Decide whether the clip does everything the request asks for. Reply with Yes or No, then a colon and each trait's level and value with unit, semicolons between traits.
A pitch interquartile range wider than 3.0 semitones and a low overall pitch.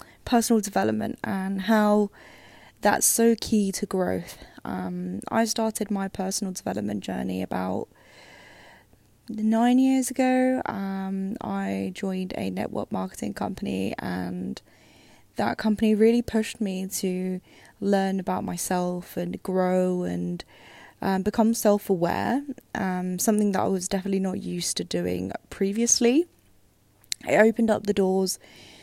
No: average, 4.0 semitones; high, 195 Hz